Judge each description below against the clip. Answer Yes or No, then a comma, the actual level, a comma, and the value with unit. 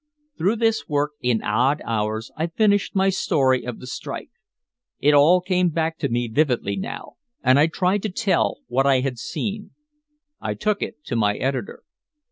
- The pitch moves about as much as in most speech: No, wide, 6.9 semitones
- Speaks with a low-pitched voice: No, medium, 145 Hz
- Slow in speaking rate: No, average, 175 wpm